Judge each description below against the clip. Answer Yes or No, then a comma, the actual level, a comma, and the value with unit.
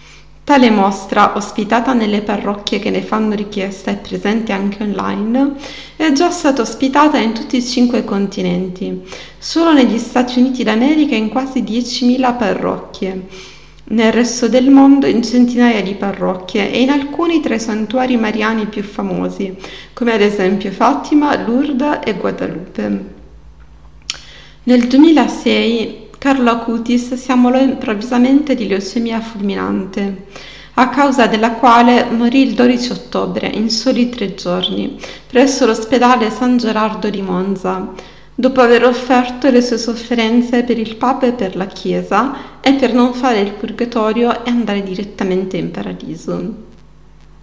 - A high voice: Yes, high, 230 Hz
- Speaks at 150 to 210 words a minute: No, average, 135 wpm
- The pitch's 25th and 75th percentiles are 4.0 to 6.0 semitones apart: No, average, 3.6 semitones